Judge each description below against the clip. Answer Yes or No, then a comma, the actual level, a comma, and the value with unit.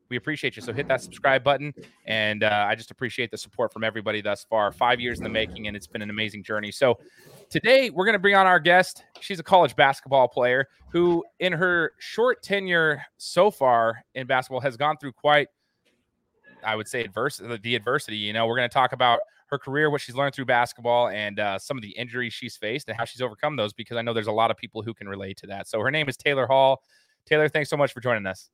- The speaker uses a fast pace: Yes, fast, 245 wpm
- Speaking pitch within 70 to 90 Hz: No, low, 125 Hz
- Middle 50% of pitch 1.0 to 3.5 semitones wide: No, average, 5.1 semitones